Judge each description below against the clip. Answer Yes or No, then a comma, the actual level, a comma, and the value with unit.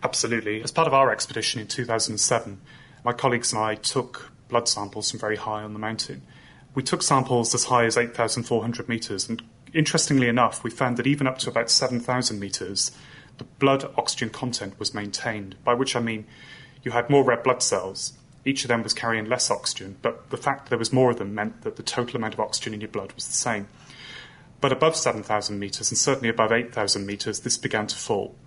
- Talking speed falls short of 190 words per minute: No, fast, 205 wpm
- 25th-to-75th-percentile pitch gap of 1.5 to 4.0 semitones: Yes, average, 3.4 semitones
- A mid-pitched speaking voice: No, low, 120 Hz